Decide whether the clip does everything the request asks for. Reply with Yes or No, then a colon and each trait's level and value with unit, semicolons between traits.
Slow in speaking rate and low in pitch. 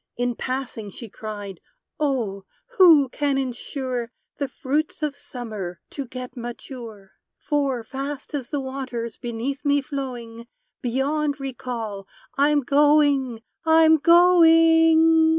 No: slow, 115 wpm; very high, 270 Hz